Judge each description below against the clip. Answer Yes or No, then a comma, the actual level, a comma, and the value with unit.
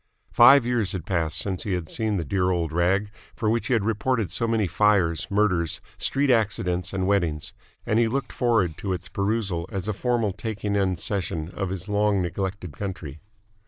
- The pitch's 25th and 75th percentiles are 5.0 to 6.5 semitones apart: No, average, 3.4 semitones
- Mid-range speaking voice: No, low, 100 Hz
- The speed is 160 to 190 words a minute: Yes, average, 185 wpm